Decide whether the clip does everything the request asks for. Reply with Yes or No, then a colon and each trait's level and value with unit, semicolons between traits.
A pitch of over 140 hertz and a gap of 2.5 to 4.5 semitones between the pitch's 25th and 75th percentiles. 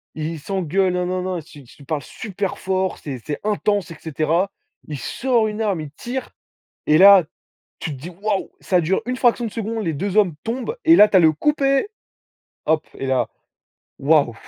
No: medium, 185 Hz; wide, 5.4 semitones